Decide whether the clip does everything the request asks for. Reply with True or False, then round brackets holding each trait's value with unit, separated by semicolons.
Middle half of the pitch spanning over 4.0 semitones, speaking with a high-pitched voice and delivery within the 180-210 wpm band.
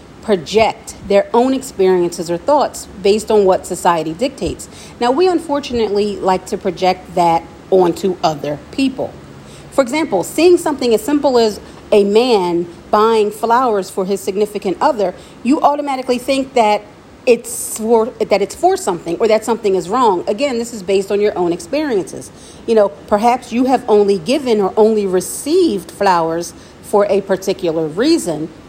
False (4.6 semitones; 210 Hz; 155 wpm)